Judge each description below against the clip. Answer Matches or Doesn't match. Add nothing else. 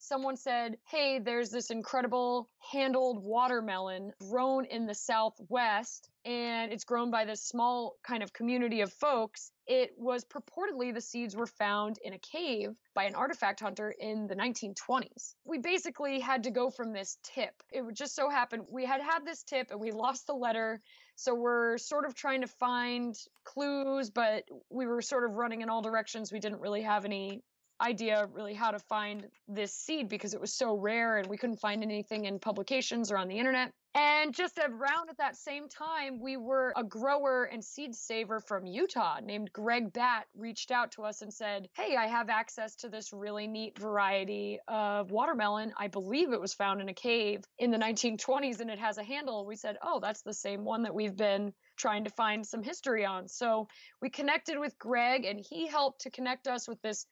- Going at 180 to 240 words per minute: Matches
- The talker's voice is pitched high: Matches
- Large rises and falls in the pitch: Doesn't match